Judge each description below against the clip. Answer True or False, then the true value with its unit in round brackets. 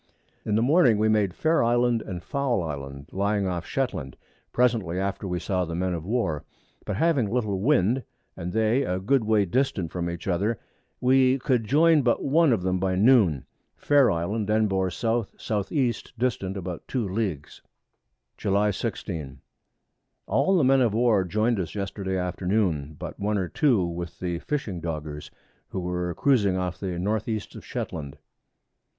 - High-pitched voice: False (100 Hz)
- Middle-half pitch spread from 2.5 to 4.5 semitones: False (5.1 semitones)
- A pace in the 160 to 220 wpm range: True (170 wpm)